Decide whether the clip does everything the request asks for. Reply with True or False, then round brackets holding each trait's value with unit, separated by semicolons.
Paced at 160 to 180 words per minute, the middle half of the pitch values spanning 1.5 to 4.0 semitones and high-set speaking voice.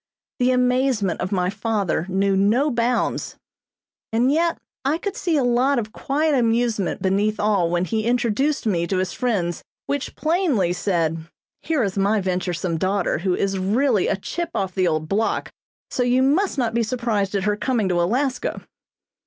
False (170 wpm; 5.1 semitones; 215 Hz)